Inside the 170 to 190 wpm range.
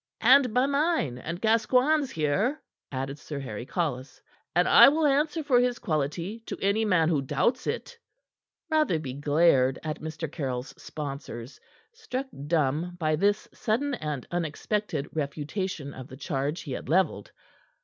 No: average, 145 wpm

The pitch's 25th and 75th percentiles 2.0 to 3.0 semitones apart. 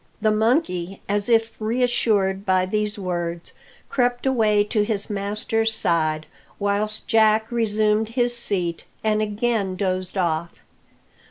Yes: average, 2.7 semitones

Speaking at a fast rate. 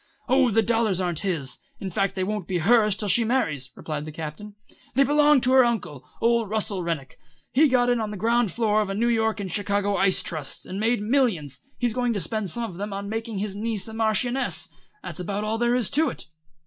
Yes: fast, 225 wpm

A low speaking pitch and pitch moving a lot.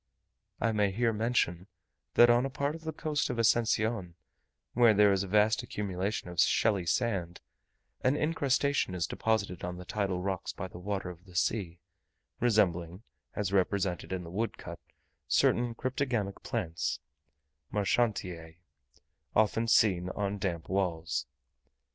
No: low, 100 Hz; average, 4.3 semitones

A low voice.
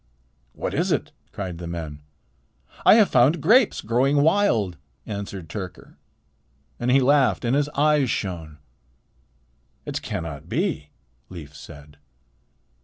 Yes: low, 110 Hz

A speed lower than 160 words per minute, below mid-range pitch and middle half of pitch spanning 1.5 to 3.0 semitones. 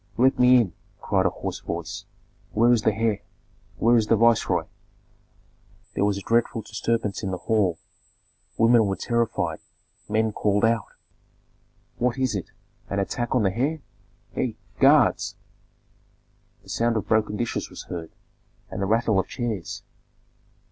Yes: average, 150 wpm; low, 110 Hz; narrow, 2.5 semitones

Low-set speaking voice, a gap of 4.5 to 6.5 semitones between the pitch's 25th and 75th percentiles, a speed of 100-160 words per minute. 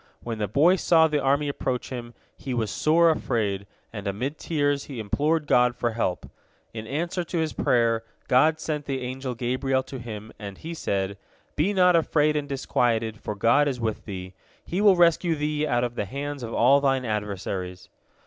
No: low, 130 Hz; average, 5.2 semitones; average, 185 wpm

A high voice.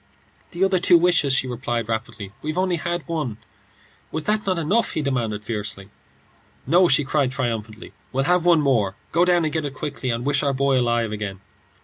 No: medium, 140 Hz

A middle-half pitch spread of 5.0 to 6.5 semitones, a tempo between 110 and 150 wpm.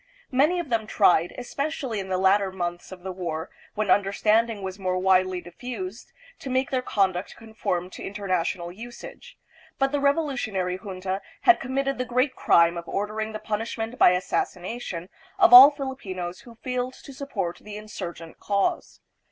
No: wide, 5.4 semitones; average, 160 wpm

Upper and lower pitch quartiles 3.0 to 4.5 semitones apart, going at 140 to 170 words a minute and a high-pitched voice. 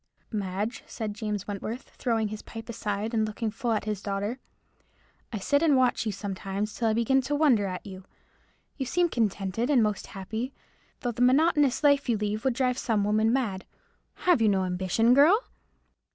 No: average, 3.8 semitones; average, 180 wpm; high, 220 Hz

